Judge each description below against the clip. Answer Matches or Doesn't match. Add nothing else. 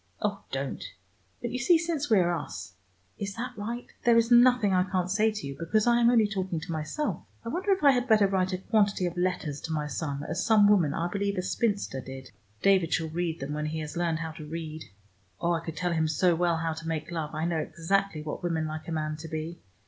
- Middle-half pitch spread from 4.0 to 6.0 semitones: Matches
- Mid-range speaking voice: Matches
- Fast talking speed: Matches